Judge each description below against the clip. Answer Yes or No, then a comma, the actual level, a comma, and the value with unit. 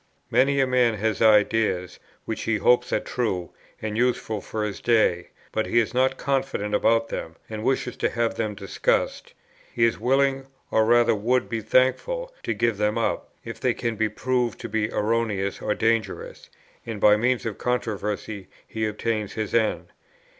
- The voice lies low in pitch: Yes, low, 115 Hz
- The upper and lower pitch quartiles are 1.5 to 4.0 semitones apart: Yes, average, 2.7 semitones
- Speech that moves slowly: No, average, 175 wpm